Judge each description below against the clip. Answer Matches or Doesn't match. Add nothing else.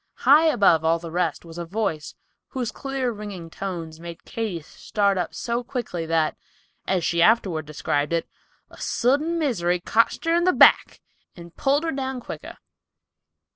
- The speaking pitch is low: Doesn't match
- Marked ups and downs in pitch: Matches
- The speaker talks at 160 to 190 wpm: Matches